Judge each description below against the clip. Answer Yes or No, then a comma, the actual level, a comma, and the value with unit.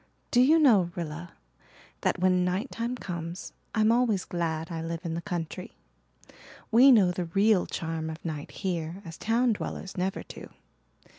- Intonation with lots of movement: No, average, 4.7 semitones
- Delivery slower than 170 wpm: Yes, average, 160 wpm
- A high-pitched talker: No, medium, 180 Hz